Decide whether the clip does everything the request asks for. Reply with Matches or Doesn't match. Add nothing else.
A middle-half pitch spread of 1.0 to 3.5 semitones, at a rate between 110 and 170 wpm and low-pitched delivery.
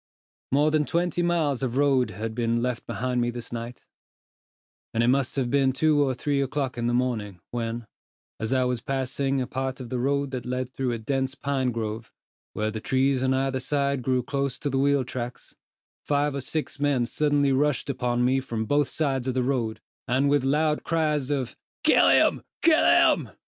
Doesn't match